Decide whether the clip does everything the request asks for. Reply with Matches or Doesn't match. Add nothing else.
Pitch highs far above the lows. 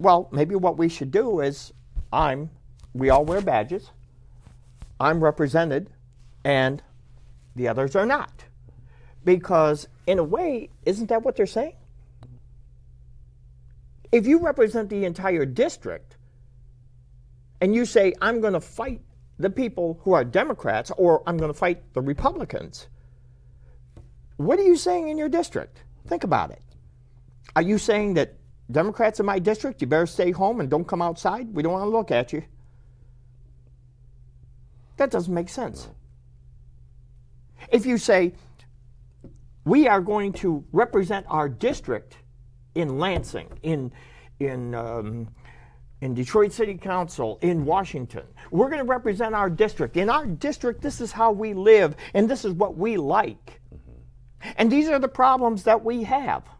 Matches